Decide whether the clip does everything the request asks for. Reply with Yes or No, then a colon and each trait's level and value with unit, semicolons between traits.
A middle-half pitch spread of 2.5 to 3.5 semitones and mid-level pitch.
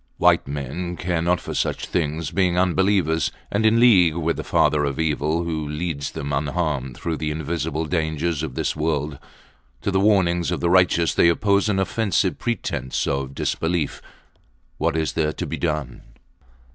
No: average, 2.9 semitones; very low, 80 Hz